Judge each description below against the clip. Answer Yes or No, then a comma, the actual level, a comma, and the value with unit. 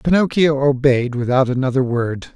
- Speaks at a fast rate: No, slow, 130 wpm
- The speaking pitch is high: No, low, 135 Hz